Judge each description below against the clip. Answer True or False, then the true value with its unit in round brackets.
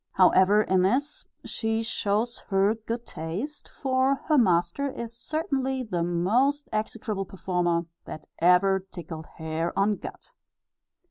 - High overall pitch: True (205 Hz)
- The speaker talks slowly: True (125 wpm)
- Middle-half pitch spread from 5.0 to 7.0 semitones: True (5.6 semitones)